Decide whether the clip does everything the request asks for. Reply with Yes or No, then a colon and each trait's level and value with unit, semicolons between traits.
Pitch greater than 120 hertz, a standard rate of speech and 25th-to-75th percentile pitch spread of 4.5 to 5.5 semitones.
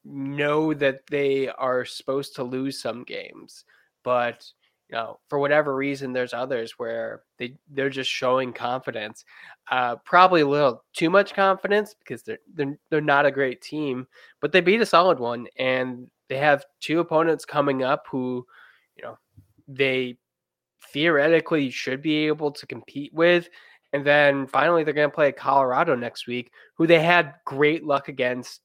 No: medium, 140 Hz; average, 165 wpm; average, 3.4 semitones